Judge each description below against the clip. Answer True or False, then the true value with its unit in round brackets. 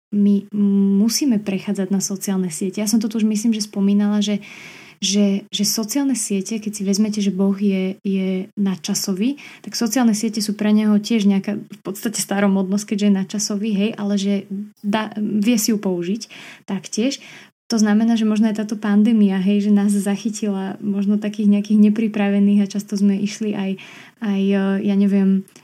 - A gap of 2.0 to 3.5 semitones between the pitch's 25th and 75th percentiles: False (1.5 semitones)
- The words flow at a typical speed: False (170 wpm)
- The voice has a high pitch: True (205 Hz)